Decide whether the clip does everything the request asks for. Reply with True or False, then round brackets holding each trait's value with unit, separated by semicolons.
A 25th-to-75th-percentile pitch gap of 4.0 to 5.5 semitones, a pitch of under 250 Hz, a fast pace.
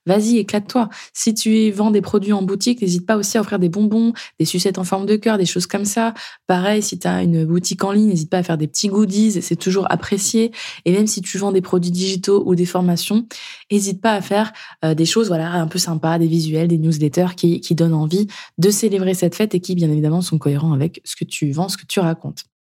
False (3.6 semitones; 190 Hz; 245 wpm)